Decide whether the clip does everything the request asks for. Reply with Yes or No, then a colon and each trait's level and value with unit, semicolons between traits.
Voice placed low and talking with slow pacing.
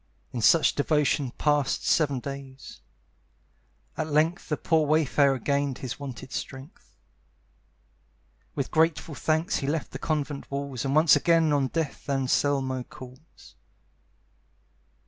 No: medium, 145 Hz; slow, 120 wpm